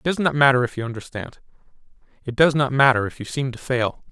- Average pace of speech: No, fast, 235 wpm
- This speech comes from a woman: No, male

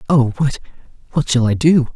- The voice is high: No, low, 135 Hz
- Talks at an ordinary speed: Yes, average, 155 wpm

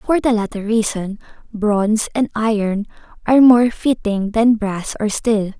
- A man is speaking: No, female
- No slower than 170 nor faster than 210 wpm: No, average, 150 wpm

